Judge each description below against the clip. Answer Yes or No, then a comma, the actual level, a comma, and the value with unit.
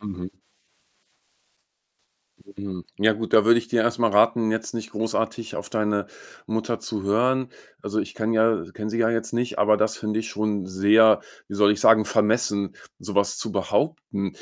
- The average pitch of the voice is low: Yes, low, 110 Hz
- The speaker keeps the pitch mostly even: Yes, narrow, 1.9 semitones